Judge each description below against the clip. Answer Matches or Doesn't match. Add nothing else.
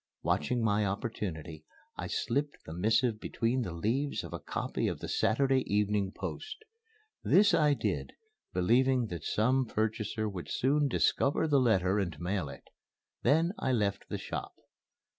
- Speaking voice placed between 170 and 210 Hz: Doesn't match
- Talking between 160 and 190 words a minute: Doesn't match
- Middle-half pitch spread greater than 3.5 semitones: Matches